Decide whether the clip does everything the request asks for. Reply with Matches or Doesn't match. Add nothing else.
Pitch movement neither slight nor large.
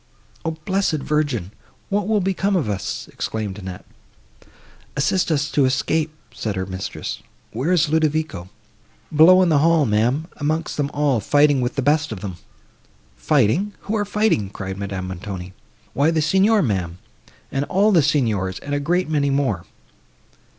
Doesn't match